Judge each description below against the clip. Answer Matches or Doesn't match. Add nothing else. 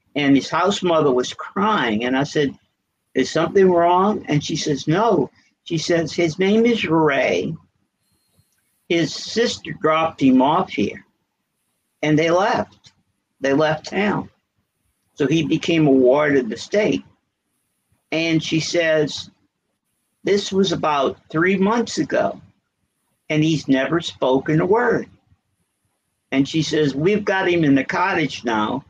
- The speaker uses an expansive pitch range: Doesn't match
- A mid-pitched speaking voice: Matches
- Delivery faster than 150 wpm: Doesn't match